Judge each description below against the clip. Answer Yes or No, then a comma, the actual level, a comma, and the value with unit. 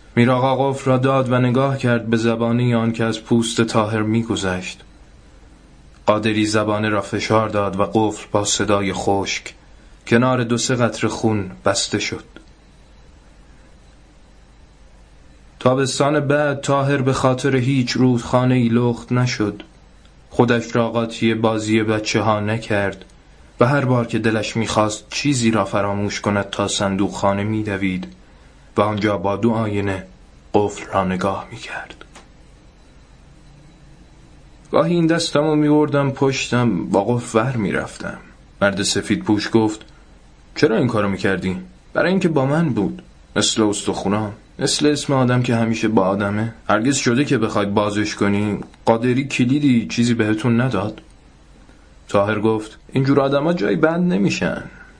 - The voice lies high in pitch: No, low, 110 Hz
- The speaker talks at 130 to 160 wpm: Yes, average, 135 wpm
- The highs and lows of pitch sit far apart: No, average, 3.8 semitones